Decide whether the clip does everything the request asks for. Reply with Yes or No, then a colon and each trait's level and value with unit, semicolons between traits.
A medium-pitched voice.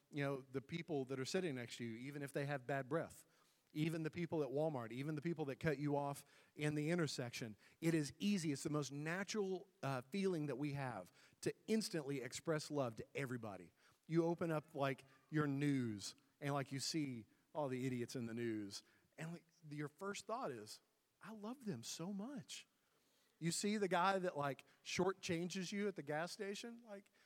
Yes: medium, 150 Hz